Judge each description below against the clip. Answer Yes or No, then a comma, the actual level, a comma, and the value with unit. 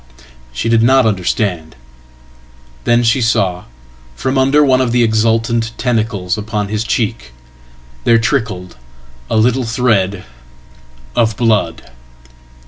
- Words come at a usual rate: No, slow, 110 wpm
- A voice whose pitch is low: Yes, low, 115 Hz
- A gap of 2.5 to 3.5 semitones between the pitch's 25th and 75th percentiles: Yes, average, 2.8 semitones